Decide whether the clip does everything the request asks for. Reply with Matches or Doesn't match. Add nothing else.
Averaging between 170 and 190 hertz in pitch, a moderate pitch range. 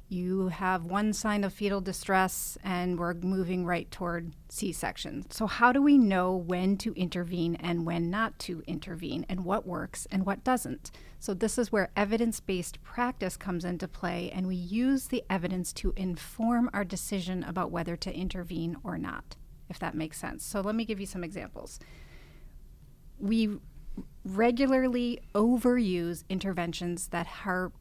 Matches